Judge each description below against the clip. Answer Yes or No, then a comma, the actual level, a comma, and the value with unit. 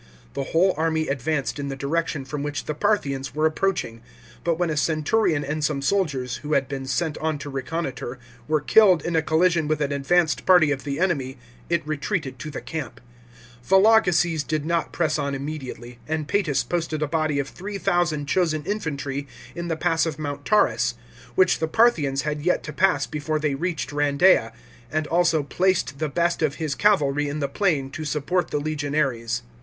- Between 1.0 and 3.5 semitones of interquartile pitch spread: Yes, average, 3.2 semitones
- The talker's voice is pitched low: No, medium, 155 Hz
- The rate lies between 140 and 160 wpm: No, average, 185 wpm